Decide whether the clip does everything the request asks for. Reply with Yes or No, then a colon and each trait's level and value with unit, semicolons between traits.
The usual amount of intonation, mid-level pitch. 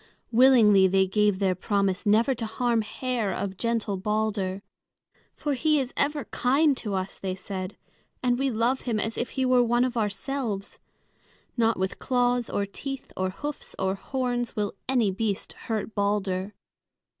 No: average, 4.0 semitones; high, 220 Hz